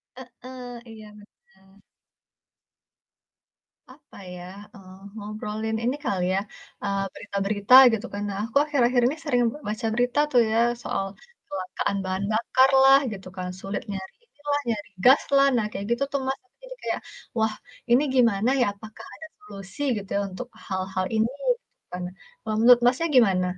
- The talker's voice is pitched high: Yes, high, 220 Hz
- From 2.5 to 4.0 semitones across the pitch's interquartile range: No, average, 4.4 semitones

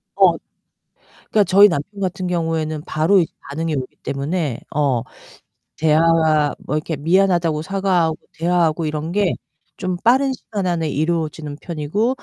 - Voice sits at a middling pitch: Yes, medium, 165 Hz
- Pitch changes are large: No, average, 3.3 semitones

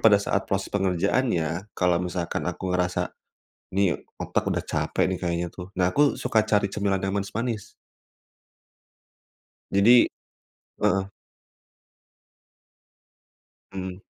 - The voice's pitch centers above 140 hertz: No, very low, 95 Hz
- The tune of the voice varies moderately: No, narrow, 2.2 semitones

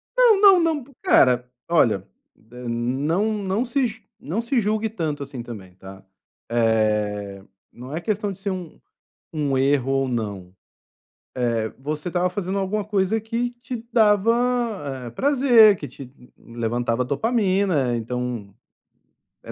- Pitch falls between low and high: Yes, medium, 165 Hz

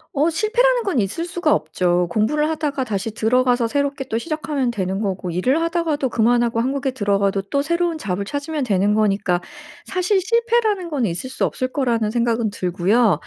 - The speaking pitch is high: Yes, very high, 250 Hz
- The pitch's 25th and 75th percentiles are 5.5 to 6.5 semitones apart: No, wide, 7.3 semitones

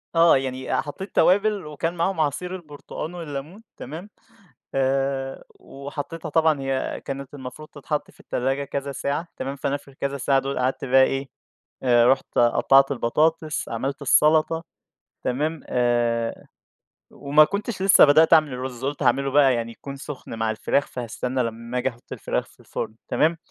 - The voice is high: No, medium, 140 Hz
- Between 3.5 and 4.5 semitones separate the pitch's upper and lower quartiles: No, average, 3.0 semitones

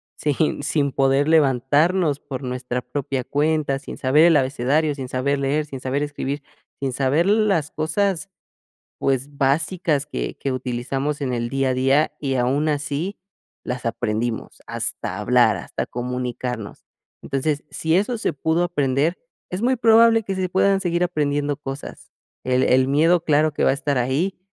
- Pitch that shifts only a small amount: No, average, 3.4 semitones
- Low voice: No, medium, 145 Hz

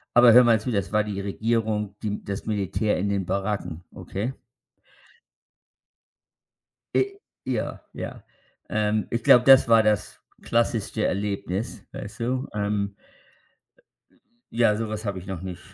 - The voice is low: Yes, low, 105 Hz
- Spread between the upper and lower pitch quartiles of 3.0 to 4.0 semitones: No, narrow, 2.5 semitones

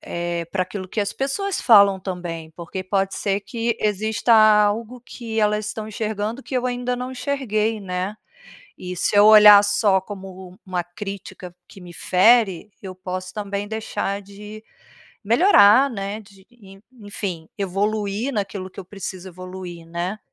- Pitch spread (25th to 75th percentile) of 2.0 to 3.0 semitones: Yes, average, 2.7 semitones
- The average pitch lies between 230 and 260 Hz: No, high, 205 Hz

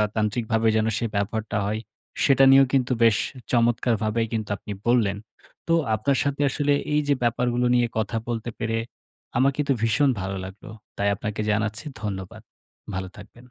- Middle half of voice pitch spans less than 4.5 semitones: Yes, average, 2.7 semitones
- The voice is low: Yes, low, 115 Hz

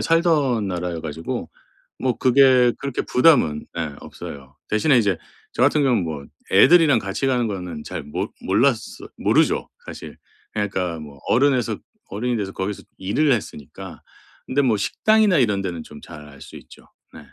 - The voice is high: No, low, 110 Hz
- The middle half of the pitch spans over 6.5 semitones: Yes, wide, 7.3 semitones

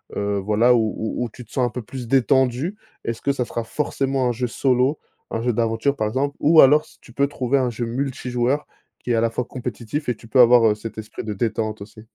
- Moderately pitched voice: No, low, 120 Hz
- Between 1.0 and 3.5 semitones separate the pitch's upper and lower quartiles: Yes, average, 2.9 semitones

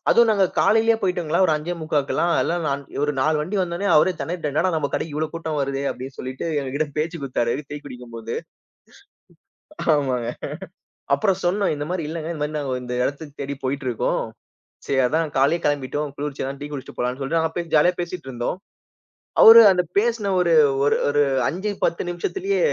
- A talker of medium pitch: Yes, medium, 150 Hz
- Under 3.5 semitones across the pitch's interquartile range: No, average, 4.0 semitones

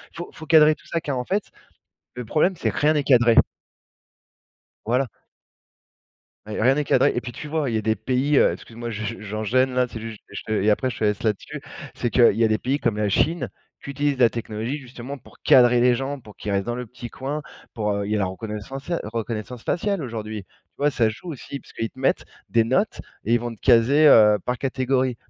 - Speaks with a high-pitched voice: No, low, 120 Hz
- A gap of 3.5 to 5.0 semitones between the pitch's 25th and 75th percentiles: Yes, average, 3.9 semitones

